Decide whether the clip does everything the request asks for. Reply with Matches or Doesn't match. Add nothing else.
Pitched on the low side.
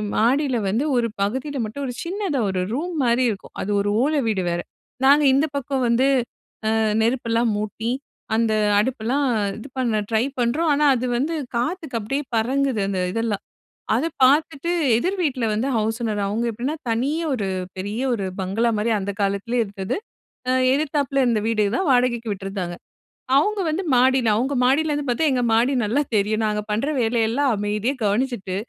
Doesn't match